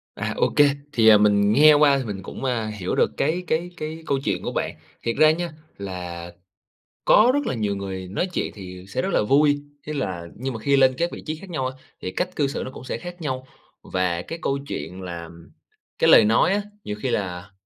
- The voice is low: Yes, low, 125 Hz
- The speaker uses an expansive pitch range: Yes, wide, 7.9 semitones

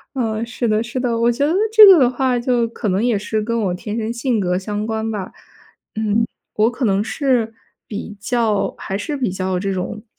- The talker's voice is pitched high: Yes, high, 225 Hz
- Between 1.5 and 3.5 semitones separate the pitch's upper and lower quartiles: Yes, average, 2.7 semitones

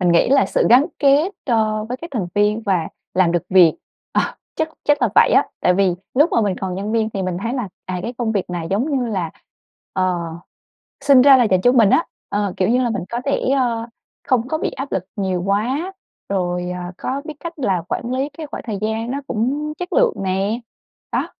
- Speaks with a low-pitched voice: No, high, 225 Hz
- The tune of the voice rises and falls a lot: Yes, wide, 5.9 semitones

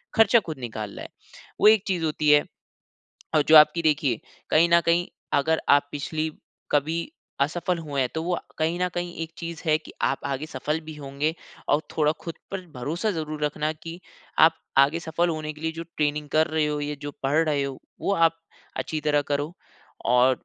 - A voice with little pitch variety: Yes, narrow, 2.3 semitones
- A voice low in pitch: No, medium, 155 Hz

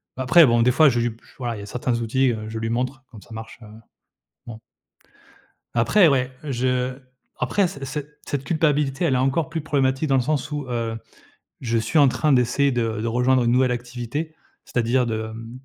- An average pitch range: Yes, average, 3.1 semitones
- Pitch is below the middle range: Yes, low, 125 Hz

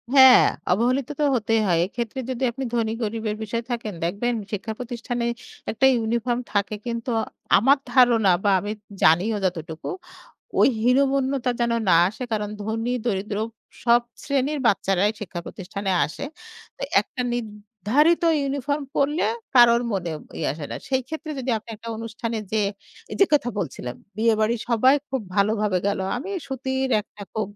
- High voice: Yes, high, 230 Hz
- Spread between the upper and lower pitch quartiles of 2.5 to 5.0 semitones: Yes, average, 3.7 semitones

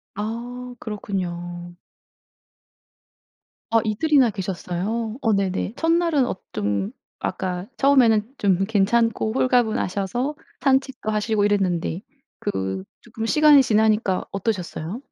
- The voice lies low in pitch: No, high, 215 Hz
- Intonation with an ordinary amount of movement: Yes, average, 4.1 semitones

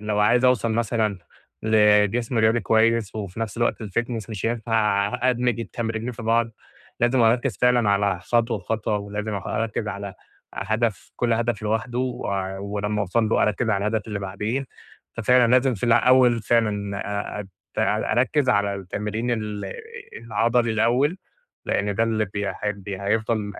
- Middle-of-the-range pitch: No, low, 110 Hz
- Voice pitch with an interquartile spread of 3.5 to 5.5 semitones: No, narrow, 2.4 semitones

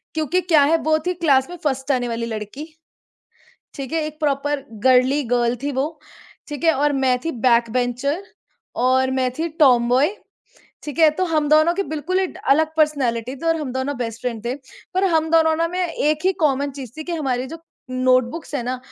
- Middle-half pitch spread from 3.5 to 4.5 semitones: Yes, average, 3.8 semitones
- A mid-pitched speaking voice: No, very high, 280 Hz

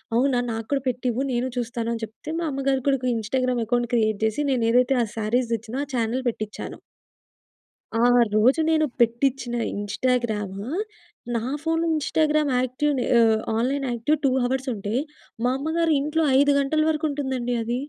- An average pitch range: Yes, average, 3.3 semitones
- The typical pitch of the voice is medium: No, very high, 250 Hz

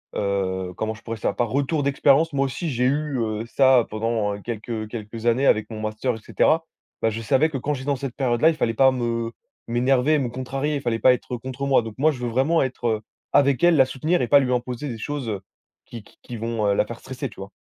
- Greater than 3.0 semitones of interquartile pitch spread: Yes, average, 3.4 semitones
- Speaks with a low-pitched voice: Yes, low, 125 Hz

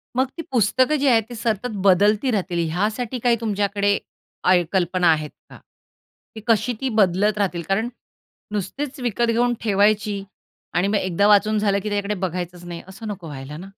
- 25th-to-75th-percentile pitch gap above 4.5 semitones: No, average, 3.4 semitones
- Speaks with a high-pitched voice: Yes, high, 205 Hz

